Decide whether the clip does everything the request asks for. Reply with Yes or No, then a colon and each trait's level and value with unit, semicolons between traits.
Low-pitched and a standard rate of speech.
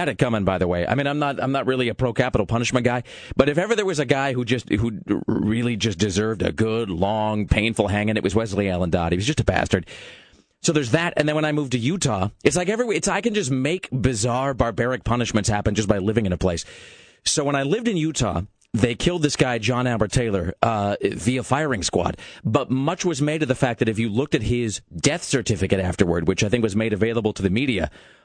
No: low, 120 Hz; fast, 245 wpm